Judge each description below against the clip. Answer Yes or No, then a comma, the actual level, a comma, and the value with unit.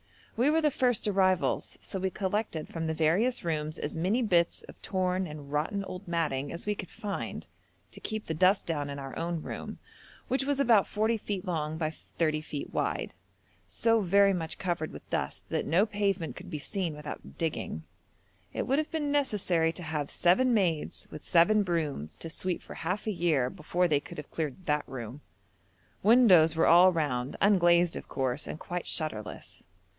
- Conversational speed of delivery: Yes, average, 185 wpm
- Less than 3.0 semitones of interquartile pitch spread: No, average, 4.6 semitones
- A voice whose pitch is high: No, medium, 175 Hz